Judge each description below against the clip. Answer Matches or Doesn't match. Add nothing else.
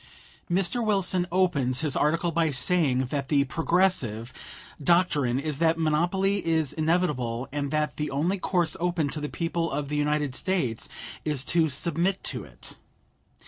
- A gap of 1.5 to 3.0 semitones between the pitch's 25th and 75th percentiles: Doesn't match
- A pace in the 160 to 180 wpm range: Doesn't match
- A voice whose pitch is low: Doesn't match